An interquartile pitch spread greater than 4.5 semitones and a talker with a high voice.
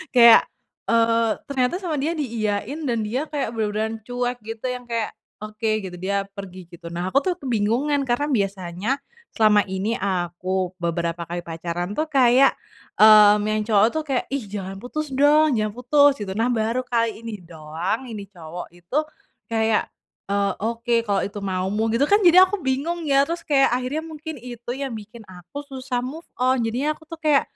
Yes: average, 5.0 semitones; high, 230 Hz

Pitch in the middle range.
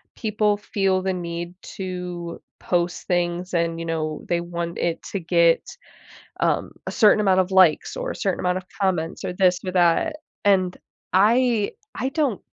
Yes: medium, 180 Hz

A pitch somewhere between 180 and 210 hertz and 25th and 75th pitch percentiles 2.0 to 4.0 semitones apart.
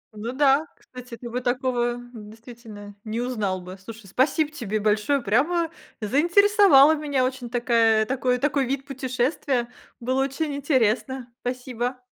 No: very high, 250 Hz; average, 3.2 semitones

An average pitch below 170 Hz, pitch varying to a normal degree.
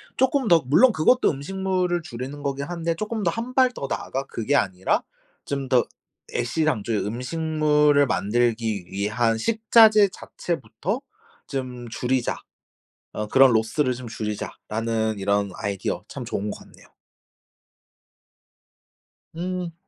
No: low, 135 Hz; wide, 7.5 semitones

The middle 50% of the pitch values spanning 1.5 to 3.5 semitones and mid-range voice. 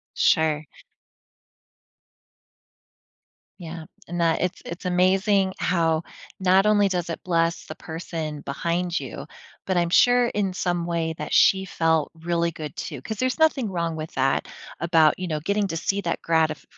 Yes: average, 2.7 semitones; medium, 170 Hz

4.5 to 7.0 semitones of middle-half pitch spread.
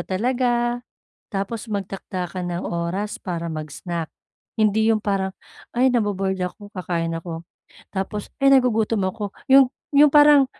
Yes: average, 4.9 semitones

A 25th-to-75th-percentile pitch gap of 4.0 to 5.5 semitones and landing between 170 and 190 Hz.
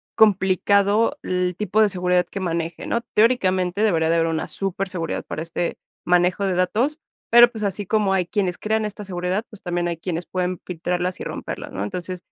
No: average, 2.9 semitones; medium, 185 Hz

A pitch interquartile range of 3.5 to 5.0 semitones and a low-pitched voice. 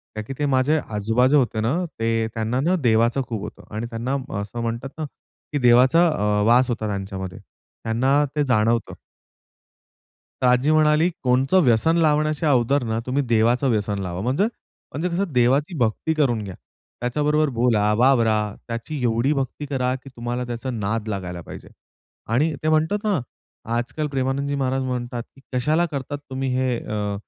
Yes: average, 4.1 semitones; low, 125 Hz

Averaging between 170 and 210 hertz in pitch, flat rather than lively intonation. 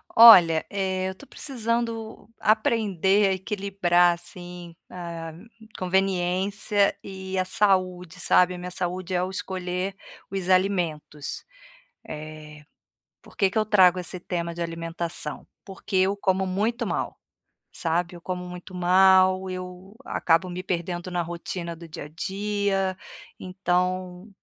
Yes: medium, 185 Hz; narrow, 1.8 semitones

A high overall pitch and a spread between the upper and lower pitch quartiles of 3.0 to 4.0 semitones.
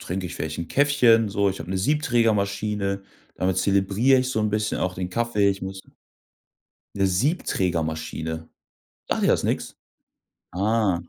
No: low, 100 Hz; average, 3.6 semitones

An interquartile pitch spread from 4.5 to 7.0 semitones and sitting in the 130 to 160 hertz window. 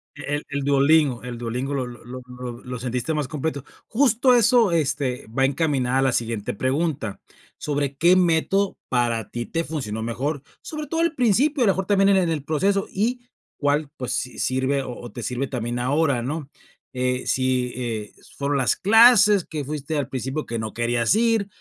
Yes: wide, 5.5 semitones; medium, 140 Hz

